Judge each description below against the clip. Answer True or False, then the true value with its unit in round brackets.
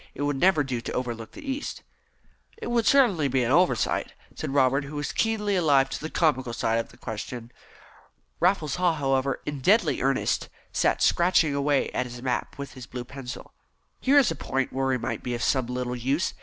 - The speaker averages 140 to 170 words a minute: False (200 wpm)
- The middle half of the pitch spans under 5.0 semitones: False (5.3 semitones)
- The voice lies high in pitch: False (140 Hz)